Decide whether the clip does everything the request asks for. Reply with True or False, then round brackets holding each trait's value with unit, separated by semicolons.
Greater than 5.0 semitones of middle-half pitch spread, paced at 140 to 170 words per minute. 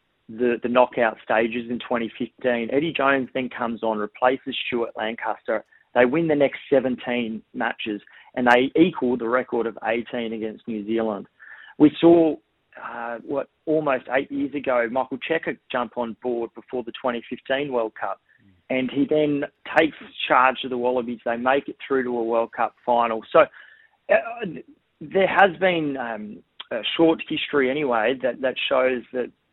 False (3.2 semitones; 160 wpm)